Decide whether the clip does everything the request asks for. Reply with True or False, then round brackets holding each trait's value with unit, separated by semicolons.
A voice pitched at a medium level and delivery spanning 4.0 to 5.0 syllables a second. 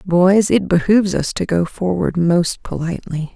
True (180 Hz; 4.6 syllables/s)